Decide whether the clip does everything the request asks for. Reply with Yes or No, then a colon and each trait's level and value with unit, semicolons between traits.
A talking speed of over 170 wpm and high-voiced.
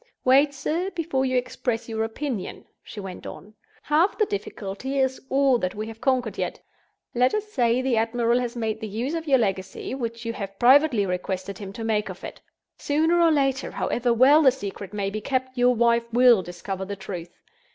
Yes: average, 195 wpm; high, 240 Hz